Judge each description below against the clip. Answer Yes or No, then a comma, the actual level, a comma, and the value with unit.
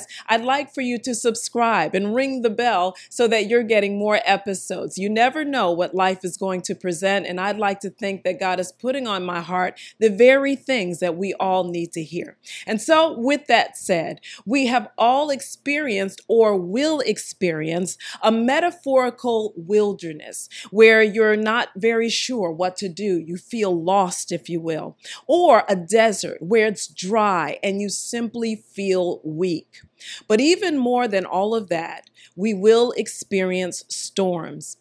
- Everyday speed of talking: Yes, average, 165 wpm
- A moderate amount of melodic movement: Yes, average, 4.4 semitones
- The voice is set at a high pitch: Yes, high, 205 Hz